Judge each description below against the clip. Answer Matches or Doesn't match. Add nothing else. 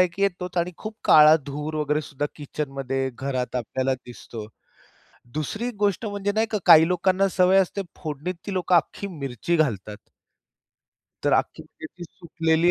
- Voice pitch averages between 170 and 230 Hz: Doesn't match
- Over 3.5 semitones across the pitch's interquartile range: Matches